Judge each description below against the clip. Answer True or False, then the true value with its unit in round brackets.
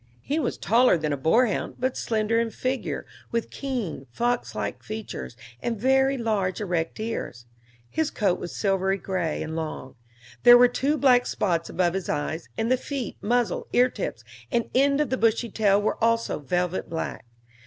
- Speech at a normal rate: True (175 wpm)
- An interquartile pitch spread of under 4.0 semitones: False (5.5 semitones)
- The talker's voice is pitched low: False (225 Hz)